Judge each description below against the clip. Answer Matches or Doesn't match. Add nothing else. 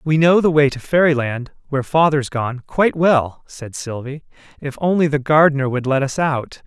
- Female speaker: Doesn't match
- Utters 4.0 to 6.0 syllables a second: Matches